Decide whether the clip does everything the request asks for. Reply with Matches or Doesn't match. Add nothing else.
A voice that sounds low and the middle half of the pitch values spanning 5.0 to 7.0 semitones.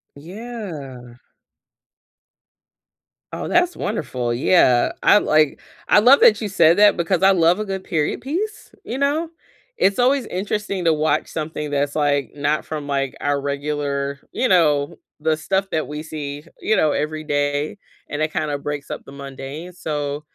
Doesn't match